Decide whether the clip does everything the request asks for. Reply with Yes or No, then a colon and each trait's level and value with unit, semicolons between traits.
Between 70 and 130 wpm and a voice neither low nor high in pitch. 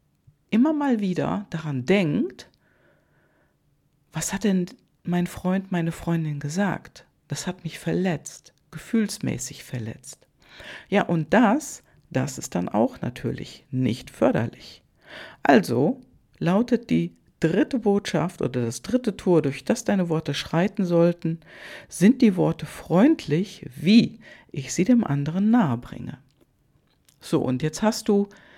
Yes: slow, 125 wpm; medium, 170 Hz